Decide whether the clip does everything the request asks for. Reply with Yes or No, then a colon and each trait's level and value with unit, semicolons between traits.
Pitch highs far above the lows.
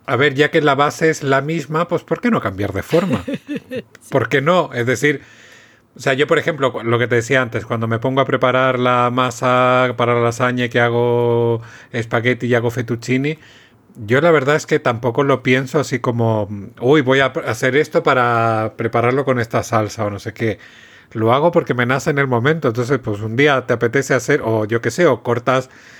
No: average, 3.4 semitones